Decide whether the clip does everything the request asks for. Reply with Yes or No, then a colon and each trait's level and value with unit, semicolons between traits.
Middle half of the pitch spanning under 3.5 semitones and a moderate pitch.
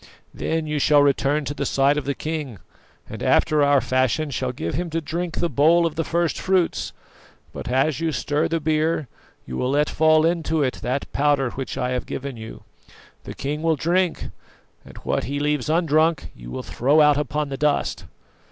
Yes: average, 2.8 semitones; medium, 150 Hz